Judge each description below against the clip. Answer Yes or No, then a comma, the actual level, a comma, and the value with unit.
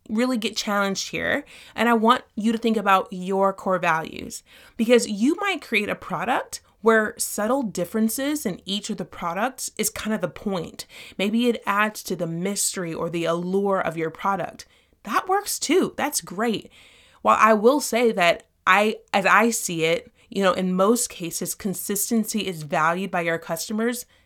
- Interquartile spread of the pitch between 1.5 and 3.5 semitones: No, average, 4.0 semitones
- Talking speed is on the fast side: No, average, 175 wpm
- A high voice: Yes, high, 210 Hz